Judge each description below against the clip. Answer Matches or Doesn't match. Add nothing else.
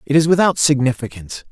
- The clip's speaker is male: Matches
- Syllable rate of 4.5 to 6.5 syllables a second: Doesn't match